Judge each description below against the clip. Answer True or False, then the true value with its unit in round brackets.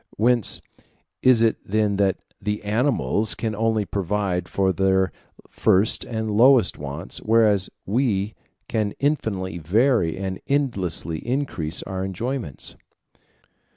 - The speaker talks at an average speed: False (115 wpm)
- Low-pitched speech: True (105 Hz)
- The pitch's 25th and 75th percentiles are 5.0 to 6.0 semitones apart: False (3.3 semitones)